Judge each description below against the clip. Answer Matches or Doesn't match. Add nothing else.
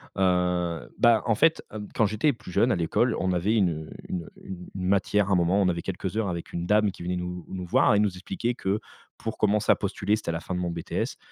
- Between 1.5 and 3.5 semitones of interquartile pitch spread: Matches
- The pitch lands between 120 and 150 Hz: Doesn't match